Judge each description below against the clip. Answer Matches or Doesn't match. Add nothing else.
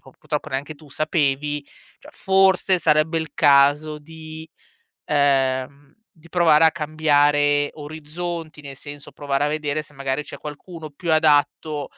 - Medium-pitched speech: Matches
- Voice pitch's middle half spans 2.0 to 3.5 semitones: Doesn't match